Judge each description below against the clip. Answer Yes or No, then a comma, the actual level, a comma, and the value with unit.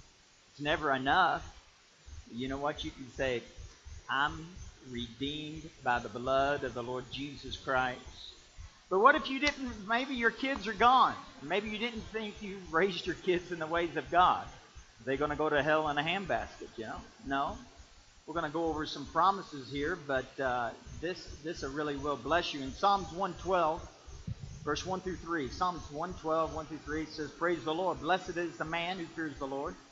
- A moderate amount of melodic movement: Yes, average, 4.5 semitones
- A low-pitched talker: No, medium, 155 Hz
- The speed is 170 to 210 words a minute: Yes, average, 190 wpm